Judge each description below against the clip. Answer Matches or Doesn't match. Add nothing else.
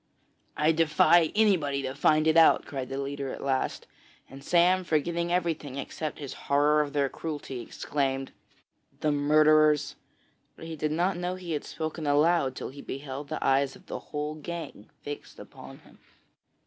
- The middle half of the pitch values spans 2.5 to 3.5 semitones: Matches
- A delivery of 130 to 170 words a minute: Matches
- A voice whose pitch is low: Doesn't match